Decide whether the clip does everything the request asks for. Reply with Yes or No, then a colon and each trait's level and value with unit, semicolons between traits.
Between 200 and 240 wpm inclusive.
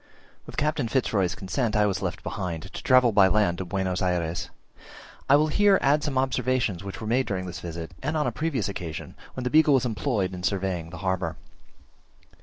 Yes: fast, 205 wpm